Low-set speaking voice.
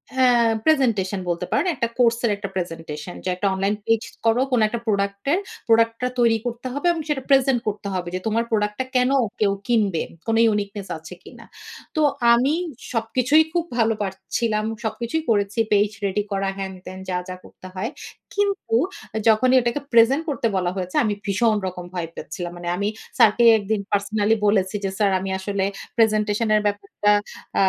No: high, 215 Hz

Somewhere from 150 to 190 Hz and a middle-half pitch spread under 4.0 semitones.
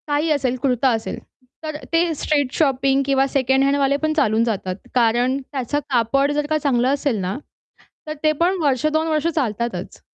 No: very high, 275 Hz; average, 3.4 semitones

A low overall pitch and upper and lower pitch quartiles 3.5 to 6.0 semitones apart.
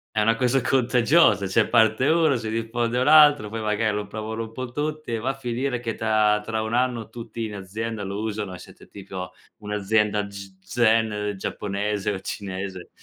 No: low, 110 Hz; narrow, 2.6 semitones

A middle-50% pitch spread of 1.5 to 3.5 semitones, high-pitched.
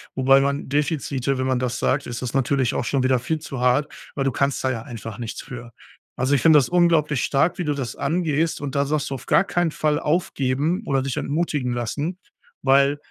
No: average, 2.7 semitones; medium, 140 Hz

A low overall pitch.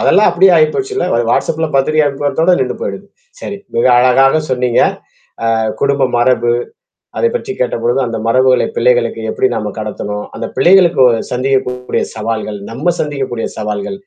Yes: low, 130 Hz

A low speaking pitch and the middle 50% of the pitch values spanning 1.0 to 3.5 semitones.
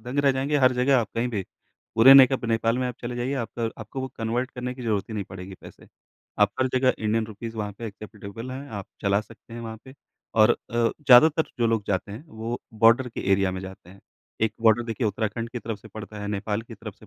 Yes: low, 115 Hz; average, 2.8 semitones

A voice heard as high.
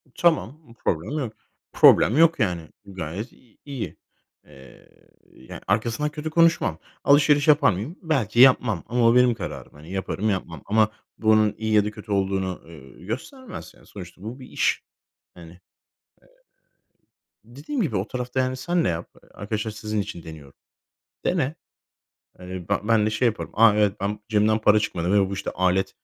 No: low, 110 Hz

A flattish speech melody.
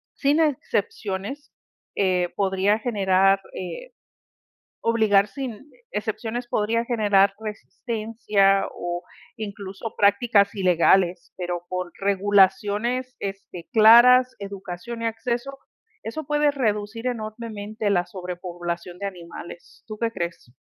No: average, 3.4 semitones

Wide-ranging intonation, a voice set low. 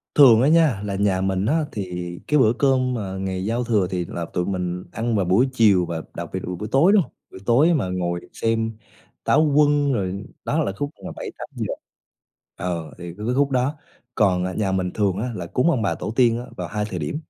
Yes: wide, 5.7 semitones; low, 105 Hz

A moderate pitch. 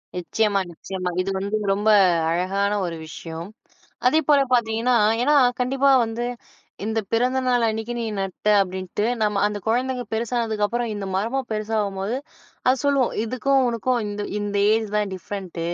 No: high, 220 Hz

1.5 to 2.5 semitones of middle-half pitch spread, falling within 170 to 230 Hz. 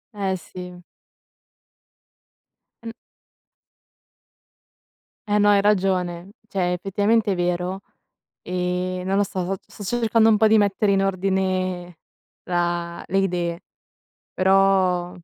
Yes: narrow, 1.8 semitones; medium, 185 Hz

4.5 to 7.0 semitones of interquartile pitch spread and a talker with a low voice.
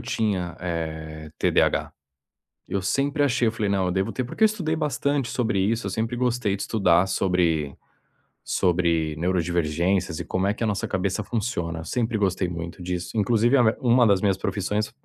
Yes: average, 4.9 semitones; very low, 95 Hz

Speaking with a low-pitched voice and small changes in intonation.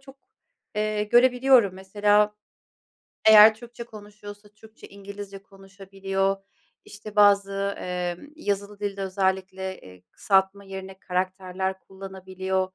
No: high, 195 Hz; narrow, 1.6 semitones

